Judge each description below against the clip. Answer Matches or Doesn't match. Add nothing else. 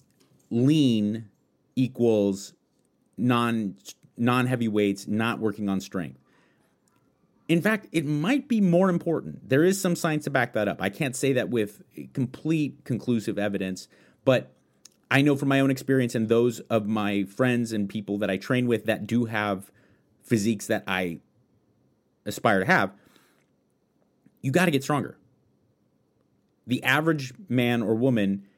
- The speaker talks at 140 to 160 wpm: Matches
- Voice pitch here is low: Matches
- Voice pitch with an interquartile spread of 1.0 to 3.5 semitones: Doesn't match